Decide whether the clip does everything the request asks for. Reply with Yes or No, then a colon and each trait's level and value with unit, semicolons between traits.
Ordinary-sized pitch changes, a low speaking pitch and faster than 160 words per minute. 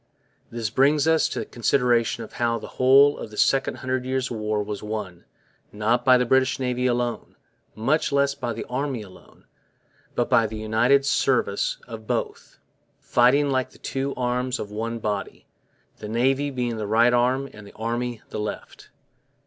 Yes: average, 3.2 semitones; low, 120 Hz; average, 175 wpm